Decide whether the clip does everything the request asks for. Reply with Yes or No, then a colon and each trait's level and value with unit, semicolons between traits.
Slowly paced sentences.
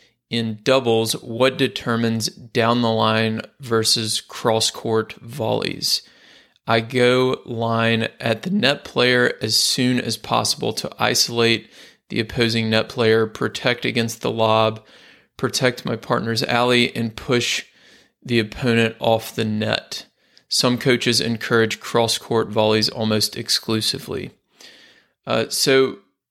Yes: slow, 120 wpm